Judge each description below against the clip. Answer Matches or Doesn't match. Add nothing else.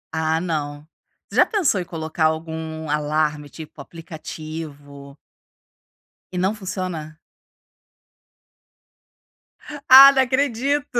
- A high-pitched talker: Doesn't match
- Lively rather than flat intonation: Doesn't match